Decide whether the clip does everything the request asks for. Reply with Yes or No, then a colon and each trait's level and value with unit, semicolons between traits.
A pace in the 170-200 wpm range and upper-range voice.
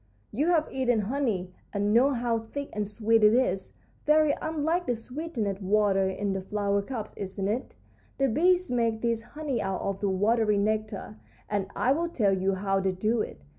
Yes: average, 185 wpm; high, 220 Hz